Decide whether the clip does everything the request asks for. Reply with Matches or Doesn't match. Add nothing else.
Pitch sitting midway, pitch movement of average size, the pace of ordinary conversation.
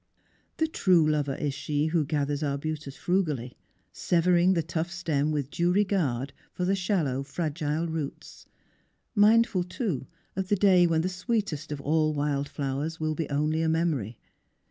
Matches